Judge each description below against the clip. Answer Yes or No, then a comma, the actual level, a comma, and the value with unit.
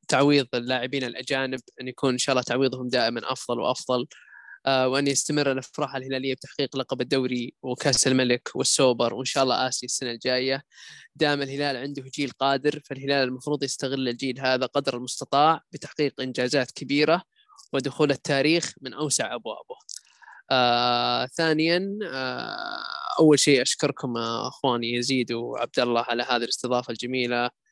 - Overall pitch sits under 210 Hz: Yes, low, 135 Hz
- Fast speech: Yes, fast, 140 wpm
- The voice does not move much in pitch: Yes, narrow, 2.2 semitones